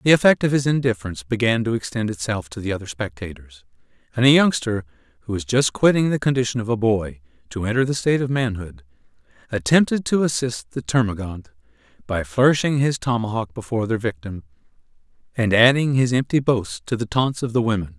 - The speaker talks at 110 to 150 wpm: No, average, 180 wpm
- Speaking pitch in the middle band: No, low, 115 Hz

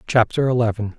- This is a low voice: Yes, low, 115 Hz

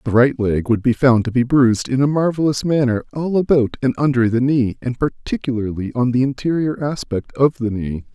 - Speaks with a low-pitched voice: Yes, low, 130 Hz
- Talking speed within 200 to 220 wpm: Yes, fast, 205 wpm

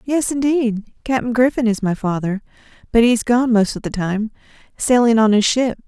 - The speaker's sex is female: Yes, female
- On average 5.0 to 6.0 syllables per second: No, 4.7 syllables/s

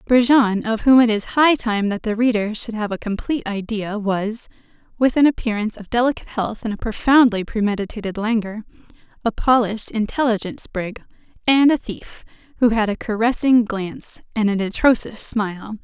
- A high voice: Yes, high, 220 Hz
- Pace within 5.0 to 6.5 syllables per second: Yes, 5.4 syllables/s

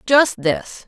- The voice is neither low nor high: No, high, 200 Hz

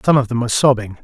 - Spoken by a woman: No, male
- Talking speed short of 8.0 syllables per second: No, 8.1 syllables/s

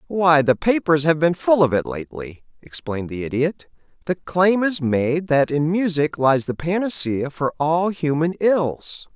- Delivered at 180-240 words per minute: No, average, 170 wpm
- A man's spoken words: Yes, male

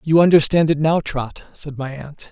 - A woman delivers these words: No, male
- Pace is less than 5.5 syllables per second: Yes, 4.6 syllables/s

